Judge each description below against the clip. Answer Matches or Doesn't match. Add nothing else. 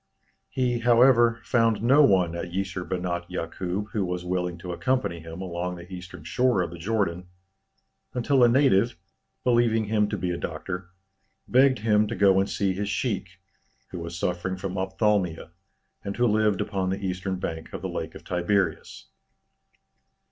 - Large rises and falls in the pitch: Doesn't match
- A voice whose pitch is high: Doesn't match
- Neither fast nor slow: Matches